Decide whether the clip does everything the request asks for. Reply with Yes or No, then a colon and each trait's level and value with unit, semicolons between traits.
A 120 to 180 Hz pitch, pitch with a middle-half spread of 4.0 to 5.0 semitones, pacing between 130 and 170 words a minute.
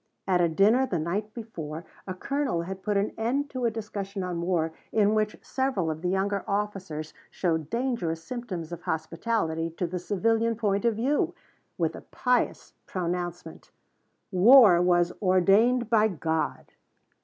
No: high, 195 Hz; average, 4.7 semitones; average, 155 wpm